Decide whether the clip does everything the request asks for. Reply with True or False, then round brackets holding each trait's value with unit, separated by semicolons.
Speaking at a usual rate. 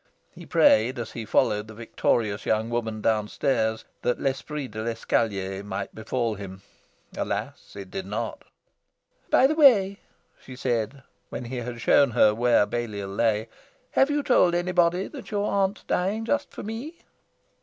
True (155 wpm)